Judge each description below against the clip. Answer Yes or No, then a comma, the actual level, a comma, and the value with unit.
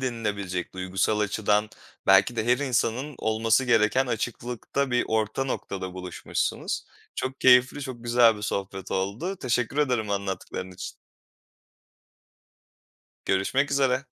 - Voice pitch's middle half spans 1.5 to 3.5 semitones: No, average, 4.4 semitones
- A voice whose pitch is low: Yes, low, 115 Hz